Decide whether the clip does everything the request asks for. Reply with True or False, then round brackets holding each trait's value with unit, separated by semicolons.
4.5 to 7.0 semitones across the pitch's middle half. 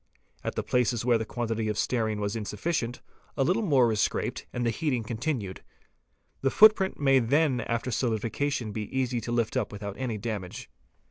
False (3.4 semitones)